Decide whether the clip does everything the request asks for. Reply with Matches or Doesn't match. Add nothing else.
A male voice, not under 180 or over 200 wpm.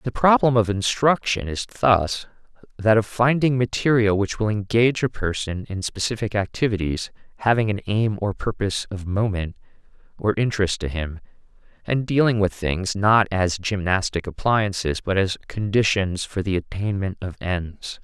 Doesn't match